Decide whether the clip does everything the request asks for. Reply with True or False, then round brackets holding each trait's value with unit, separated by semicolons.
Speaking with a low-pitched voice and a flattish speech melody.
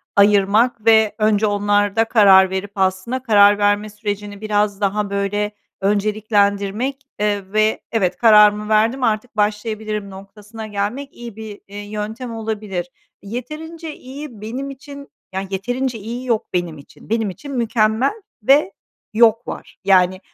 False (210 Hz; 2.2 semitones)